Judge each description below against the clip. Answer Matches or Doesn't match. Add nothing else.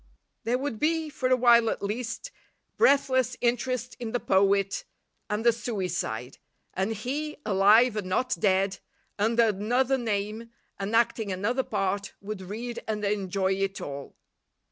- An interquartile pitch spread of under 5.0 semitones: Matches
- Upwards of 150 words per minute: Doesn't match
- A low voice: Doesn't match